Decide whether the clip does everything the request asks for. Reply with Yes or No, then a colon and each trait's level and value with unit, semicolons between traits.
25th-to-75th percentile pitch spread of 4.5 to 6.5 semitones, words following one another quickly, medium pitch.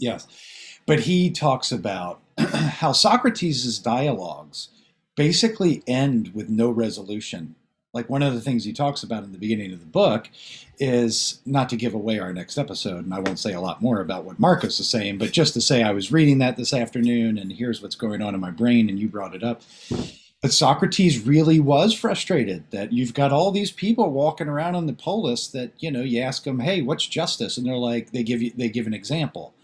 No: average, 5.0 semitones; fast, 215 wpm; low, 120 Hz